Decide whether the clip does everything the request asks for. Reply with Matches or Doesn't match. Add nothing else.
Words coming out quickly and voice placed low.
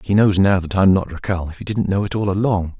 Matches